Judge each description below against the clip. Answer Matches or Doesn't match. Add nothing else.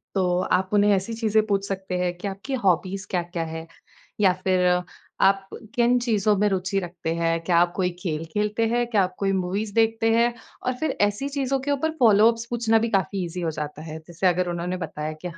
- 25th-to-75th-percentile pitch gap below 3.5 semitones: Doesn't match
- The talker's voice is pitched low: Doesn't match